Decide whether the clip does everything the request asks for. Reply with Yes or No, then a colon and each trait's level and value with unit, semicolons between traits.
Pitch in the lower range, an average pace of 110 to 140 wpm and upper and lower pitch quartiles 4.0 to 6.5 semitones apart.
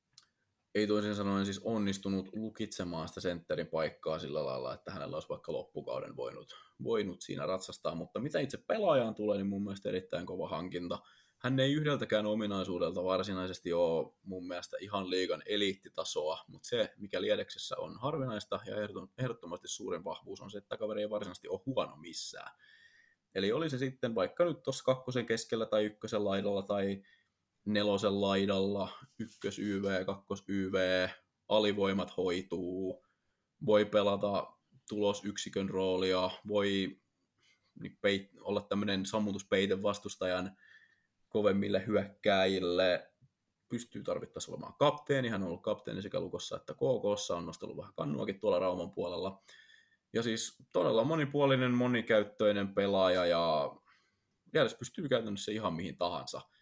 Yes: low, 105 Hz; average, 130 wpm; average, 4.6 semitones